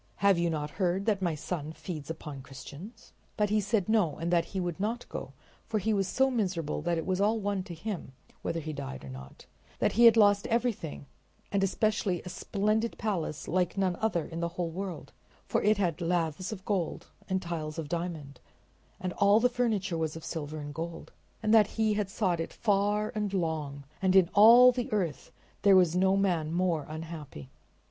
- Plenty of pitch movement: No, average, 4.3 semitones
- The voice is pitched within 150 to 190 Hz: Yes, medium, 185 Hz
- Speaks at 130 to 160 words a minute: No, average, 200 wpm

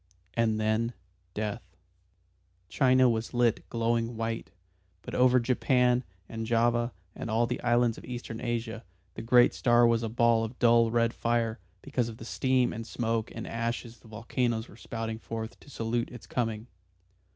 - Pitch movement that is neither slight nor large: No, narrow, 1.2 semitones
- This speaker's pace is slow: No, average, 165 wpm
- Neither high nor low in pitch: No, low, 115 Hz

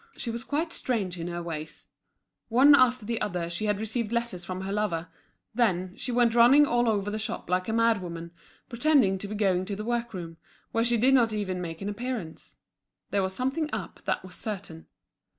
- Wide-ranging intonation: No, average, 4.6 semitones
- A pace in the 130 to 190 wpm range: No, fast, 205 wpm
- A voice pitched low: No, high, 210 Hz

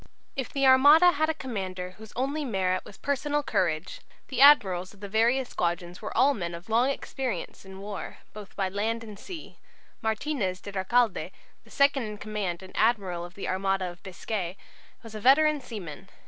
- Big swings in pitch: Yes, wide, 5.9 semitones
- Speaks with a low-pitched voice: No, high, 210 Hz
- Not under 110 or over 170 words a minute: No, average, 180 wpm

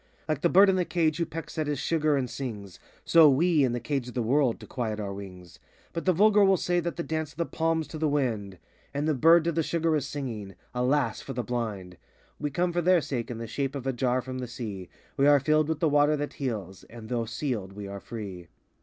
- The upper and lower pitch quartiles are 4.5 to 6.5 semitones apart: Yes, wide, 5.6 semitones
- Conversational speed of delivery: No, fast, 255 wpm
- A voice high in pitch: No, medium, 140 Hz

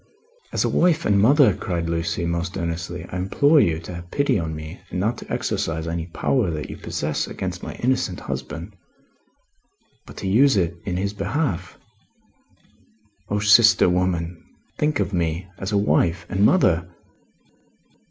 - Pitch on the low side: Yes, very low, 90 Hz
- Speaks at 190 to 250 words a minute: No, average, 160 wpm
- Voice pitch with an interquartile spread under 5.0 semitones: Yes, average, 3.9 semitones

